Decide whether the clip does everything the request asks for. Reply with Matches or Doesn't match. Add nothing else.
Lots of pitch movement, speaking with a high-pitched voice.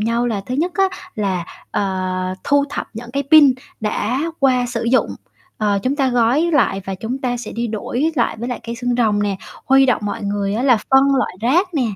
Doesn't match